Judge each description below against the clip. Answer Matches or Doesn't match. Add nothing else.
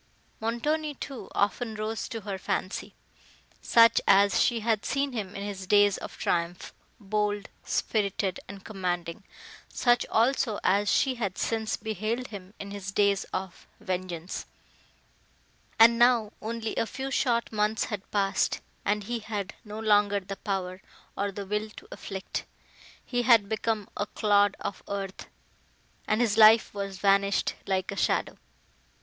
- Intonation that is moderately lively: Doesn't match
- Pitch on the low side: Doesn't match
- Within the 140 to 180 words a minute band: Matches